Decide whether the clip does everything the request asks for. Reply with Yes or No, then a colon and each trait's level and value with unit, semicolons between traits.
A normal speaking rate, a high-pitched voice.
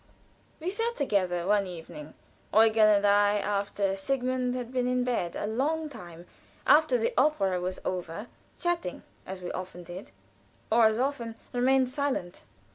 Yes: average, 150 wpm; high, 220 Hz